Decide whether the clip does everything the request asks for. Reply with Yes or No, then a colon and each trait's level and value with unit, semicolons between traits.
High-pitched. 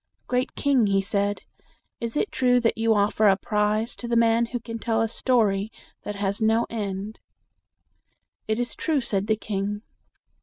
Yes: high, 220 Hz